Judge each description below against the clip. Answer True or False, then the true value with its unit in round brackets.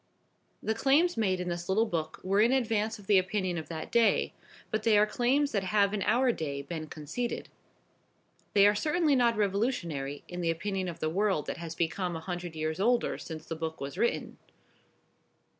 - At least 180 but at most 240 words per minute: True (190 wpm)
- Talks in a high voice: True (195 Hz)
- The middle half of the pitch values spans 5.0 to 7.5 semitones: True (5.3 semitones)